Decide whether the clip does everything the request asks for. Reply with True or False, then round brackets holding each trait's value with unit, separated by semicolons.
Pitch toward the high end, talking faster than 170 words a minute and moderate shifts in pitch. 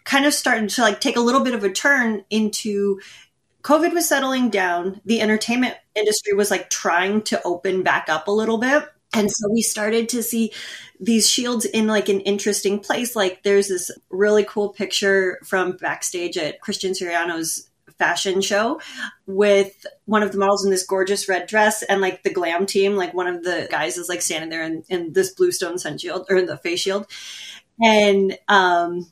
True (200 Hz; 190 wpm; 3.0 semitones)